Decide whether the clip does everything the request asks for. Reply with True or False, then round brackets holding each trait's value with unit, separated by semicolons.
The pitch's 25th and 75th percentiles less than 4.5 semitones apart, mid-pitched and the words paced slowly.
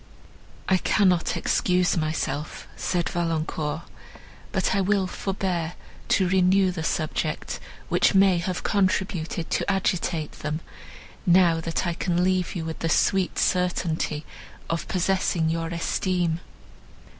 True (2.4 semitones; 175 Hz; 120 wpm)